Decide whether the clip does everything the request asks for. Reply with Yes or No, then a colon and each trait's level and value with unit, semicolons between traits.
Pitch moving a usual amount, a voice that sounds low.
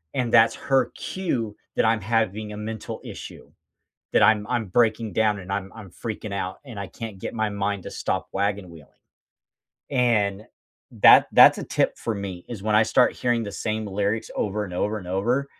No: narrow, 2.3 semitones; low, 105 Hz